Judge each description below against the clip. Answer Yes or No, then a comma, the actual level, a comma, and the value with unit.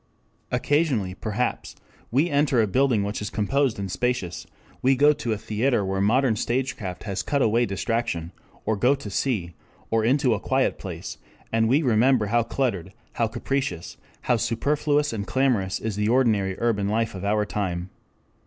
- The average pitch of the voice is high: No, low, 115 Hz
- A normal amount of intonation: Yes, average, 4.5 semitones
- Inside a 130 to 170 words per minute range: Yes, average, 165 wpm